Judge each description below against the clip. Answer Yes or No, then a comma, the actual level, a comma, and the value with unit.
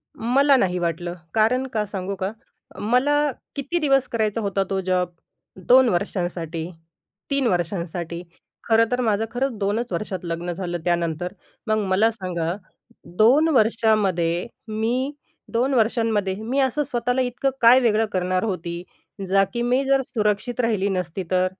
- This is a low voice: No, high, 215 Hz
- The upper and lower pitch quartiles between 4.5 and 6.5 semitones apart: Yes, average, 5.2 semitones